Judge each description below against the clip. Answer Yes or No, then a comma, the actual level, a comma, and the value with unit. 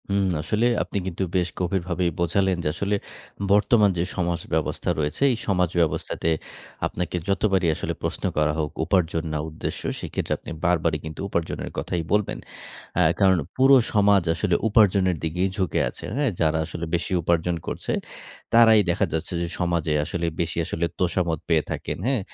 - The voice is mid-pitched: No, very low, 90 Hz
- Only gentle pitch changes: No, average, 3.1 semitones